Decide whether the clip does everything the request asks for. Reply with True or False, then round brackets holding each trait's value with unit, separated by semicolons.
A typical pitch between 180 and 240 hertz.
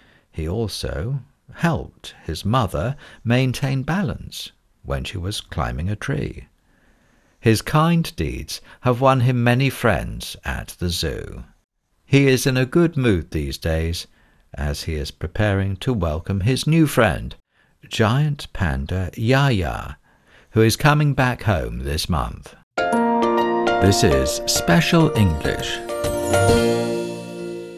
False (115 Hz)